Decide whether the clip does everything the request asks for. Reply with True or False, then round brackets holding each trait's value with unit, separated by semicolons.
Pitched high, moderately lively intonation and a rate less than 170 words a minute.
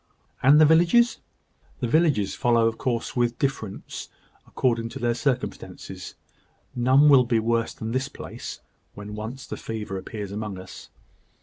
False (120 Hz; 3.6 semitones; 150 wpm)